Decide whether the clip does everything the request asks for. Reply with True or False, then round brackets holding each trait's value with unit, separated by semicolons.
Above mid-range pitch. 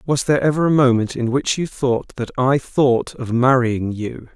False (130 Hz)